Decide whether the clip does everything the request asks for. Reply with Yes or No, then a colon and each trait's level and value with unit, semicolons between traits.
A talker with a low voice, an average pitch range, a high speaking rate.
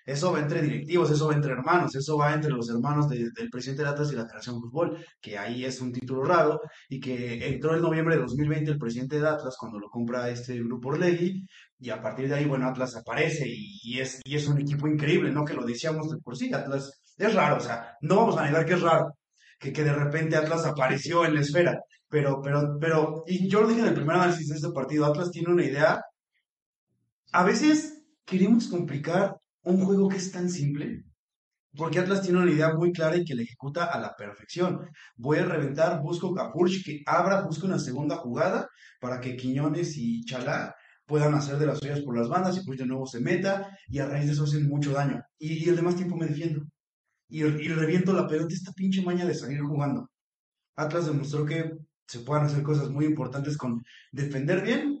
No: medium, 150 Hz; average, 4.1 semitones; fast, 220 wpm